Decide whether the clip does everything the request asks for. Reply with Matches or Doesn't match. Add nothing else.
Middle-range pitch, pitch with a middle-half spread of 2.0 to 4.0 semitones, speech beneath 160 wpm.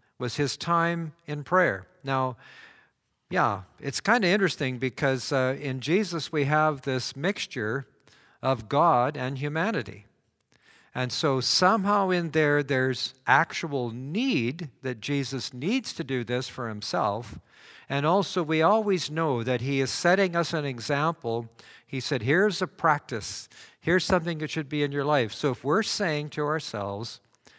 Doesn't match